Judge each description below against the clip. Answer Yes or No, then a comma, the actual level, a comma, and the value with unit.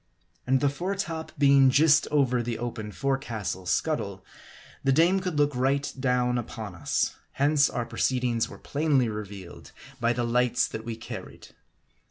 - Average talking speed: Yes, average, 160 wpm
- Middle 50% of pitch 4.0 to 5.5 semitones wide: No, average, 3.5 semitones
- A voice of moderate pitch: No, low, 125 Hz